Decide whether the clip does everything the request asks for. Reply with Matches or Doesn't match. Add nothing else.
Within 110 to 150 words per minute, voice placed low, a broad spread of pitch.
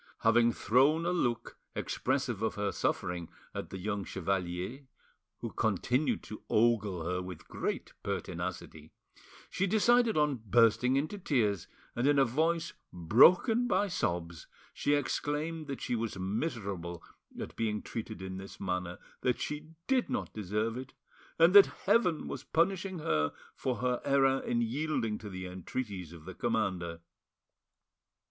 Matches